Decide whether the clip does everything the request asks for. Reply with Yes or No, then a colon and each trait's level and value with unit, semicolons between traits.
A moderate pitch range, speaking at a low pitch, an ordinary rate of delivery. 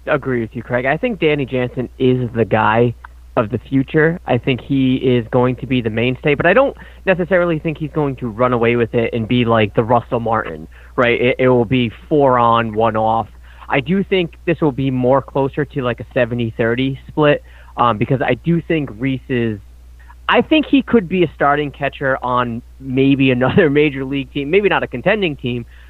No: average, 3.9 semitones; low, 130 Hz; fast, 210 wpm